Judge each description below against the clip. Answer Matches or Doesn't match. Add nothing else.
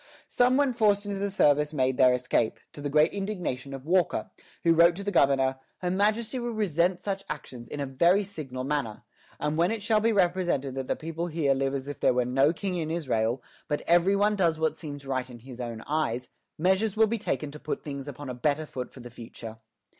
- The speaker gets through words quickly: Matches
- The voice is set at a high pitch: Doesn't match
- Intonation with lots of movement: Matches